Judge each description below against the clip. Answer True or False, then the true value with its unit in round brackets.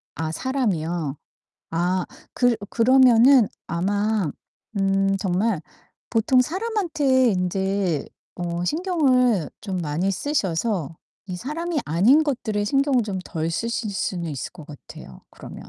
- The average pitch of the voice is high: True (200 Hz)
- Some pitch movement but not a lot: False (6.7 semitones)